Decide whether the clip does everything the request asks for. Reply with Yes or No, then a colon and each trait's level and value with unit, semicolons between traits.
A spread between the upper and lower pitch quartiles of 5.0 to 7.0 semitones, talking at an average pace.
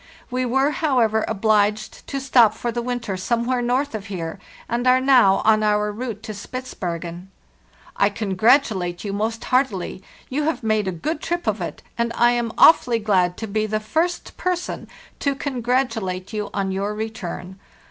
No: average, 4.0 semitones; average, 170 wpm